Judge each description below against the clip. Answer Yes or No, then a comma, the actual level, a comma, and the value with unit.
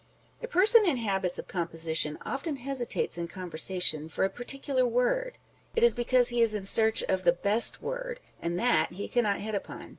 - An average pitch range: No, wide, 7.0 semitones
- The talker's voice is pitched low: No, high, 225 Hz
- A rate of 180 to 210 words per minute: Yes, average, 185 wpm